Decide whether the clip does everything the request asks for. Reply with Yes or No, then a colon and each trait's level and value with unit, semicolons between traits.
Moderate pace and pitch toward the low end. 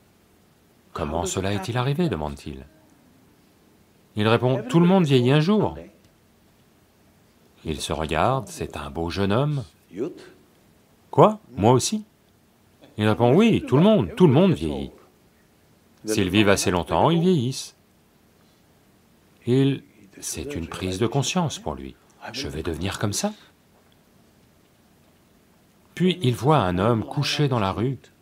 No: slow, 130 wpm; low, 110 Hz